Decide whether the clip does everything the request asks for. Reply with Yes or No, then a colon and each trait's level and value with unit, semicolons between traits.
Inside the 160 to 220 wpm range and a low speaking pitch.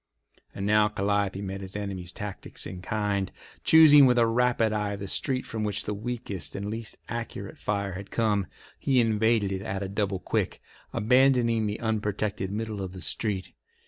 Yes: average, 175 wpm; low, 105 Hz